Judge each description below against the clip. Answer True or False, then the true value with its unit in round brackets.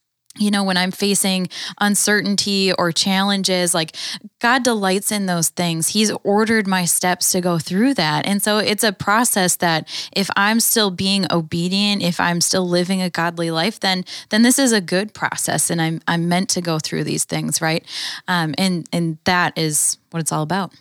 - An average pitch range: True (3.1 semitones)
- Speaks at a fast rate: False (190 wpm)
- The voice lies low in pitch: False (185 Hz)